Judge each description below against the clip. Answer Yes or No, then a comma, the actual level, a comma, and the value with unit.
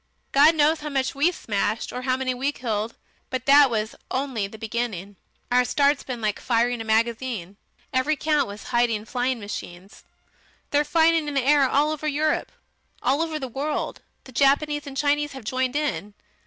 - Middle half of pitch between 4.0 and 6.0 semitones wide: Yes, average, 4.3 semitones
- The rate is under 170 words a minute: No, average, 180 wpm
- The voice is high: Yes, very high, 260 Hz